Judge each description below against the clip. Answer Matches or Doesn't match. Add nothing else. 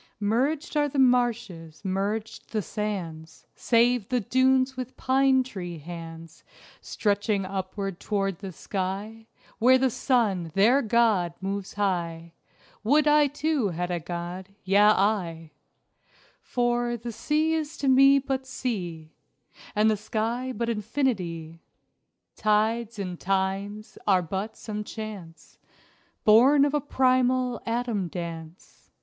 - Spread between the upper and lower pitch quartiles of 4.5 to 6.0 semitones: Matches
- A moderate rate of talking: Doesn't match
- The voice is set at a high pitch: Matches